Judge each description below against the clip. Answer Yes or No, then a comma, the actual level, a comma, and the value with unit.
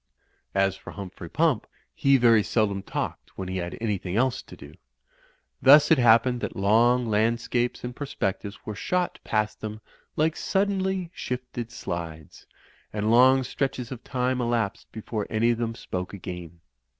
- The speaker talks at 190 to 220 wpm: No, average, 150 wpm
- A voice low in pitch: Yes, low, 115 Hz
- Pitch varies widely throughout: No, average, 4.2 semitones